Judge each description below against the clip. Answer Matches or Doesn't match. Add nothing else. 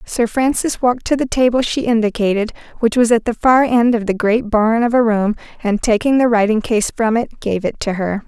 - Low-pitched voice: Doesn't match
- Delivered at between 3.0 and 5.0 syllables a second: Doesn't match